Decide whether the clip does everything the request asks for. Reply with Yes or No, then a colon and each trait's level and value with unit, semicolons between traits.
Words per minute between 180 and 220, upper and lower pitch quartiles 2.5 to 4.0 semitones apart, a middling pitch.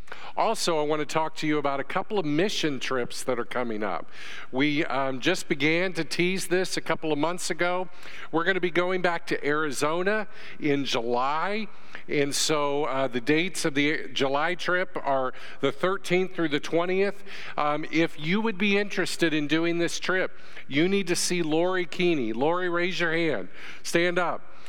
Yes: average, 185 wpm; average, 3.5 semitones; medium, 165 Hz